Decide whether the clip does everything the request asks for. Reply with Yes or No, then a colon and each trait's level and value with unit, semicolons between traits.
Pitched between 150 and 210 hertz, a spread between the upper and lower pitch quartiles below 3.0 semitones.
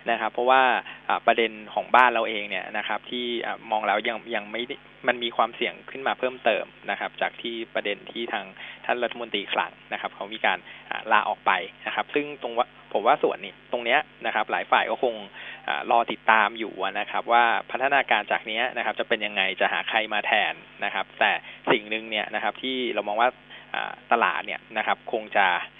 No: low, 115 Hz; narrow, 2.4 semitones